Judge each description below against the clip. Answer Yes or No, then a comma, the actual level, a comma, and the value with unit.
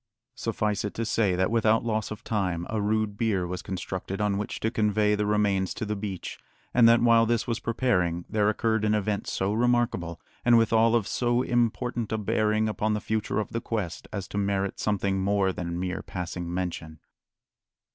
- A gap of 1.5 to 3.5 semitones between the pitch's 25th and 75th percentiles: Yes, average, 2.7 semitones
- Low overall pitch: Yes, low, 105 Hz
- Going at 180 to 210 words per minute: Yes, average, 190 wpm